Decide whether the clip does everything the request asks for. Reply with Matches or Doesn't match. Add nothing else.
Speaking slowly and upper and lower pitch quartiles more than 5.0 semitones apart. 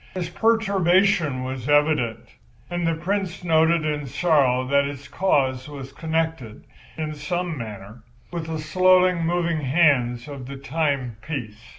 Doesn't match